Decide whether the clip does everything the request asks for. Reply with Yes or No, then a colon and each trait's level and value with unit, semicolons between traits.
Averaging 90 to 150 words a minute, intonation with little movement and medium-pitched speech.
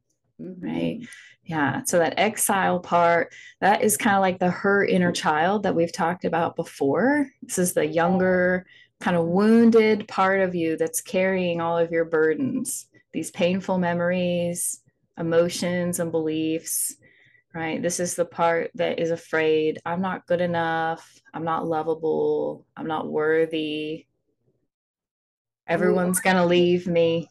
Yes: average, 145 wpm; narrow, 2.2 semitones; medium, 170 Hz